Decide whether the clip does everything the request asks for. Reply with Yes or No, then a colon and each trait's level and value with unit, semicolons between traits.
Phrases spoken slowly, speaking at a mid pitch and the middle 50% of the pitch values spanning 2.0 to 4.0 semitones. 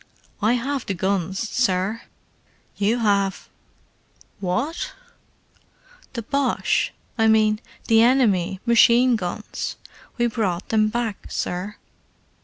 No: slow, 90 wpm; high, 220 Hz; average, 3.6 semitones